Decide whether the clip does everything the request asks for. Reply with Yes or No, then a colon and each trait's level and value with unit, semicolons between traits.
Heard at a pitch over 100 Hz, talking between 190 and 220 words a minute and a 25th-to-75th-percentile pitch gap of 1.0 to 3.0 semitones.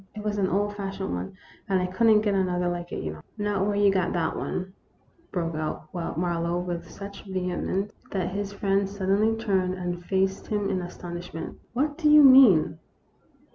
Yes: high, 190 Hz; fast, 205 wpm; average, 2.7 semitones